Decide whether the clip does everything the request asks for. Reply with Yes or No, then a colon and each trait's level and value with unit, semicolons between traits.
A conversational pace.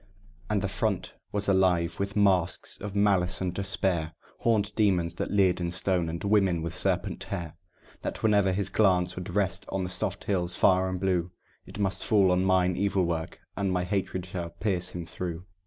Yes: average, 190 wpm